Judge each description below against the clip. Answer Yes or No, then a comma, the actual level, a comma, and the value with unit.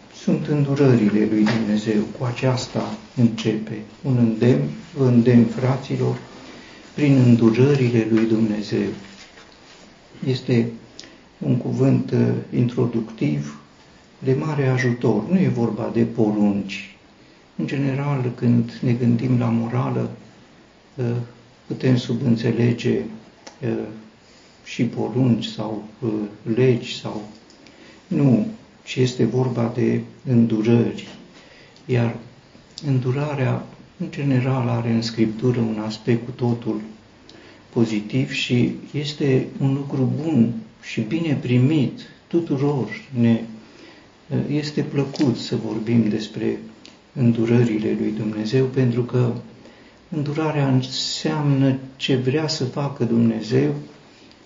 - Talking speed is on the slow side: Yes, slow, 100 wpm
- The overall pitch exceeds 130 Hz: No, low, 120 Hz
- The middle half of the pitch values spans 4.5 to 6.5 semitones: No, average, 2.9 semitones